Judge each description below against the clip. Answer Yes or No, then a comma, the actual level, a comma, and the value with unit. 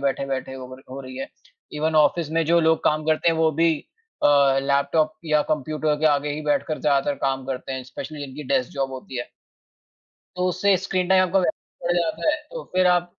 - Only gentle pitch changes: No, average, 3.7 semitones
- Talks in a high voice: No, medium, 155 Hz